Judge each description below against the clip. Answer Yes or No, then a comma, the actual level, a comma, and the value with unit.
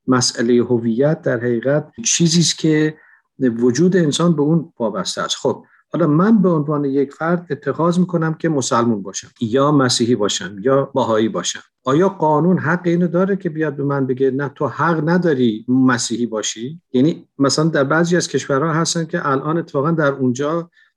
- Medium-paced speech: No, fast, 170 wpm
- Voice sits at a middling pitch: Yes, medium, 145 Hz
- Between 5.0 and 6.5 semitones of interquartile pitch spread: No, average, 4.3 semitones